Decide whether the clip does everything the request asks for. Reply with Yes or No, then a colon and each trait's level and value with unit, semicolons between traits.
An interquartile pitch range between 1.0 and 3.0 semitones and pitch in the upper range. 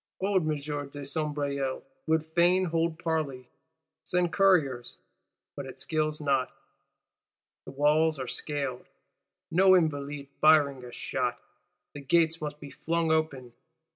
No: average, 2.7 semitones; medium, 150 Hz